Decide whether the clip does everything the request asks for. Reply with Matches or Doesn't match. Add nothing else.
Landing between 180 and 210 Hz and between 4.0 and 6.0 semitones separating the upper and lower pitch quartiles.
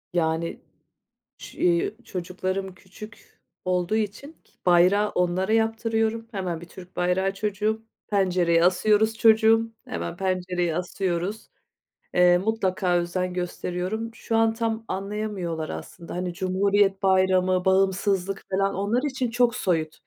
Doesn't match